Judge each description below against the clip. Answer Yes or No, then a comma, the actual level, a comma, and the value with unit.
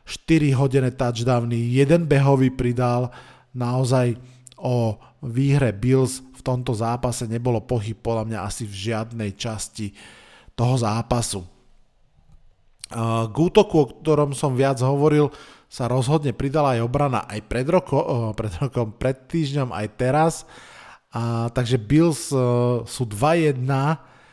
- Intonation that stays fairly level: No, average, 3.1 semitones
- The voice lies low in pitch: Yes, low, 125 Hz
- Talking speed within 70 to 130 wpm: Yes, average, 120 wpm